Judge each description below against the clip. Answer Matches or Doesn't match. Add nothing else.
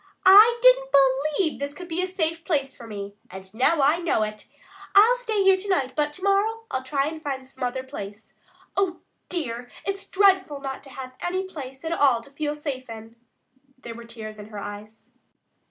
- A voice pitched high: Matches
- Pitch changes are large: Matches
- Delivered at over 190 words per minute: Matches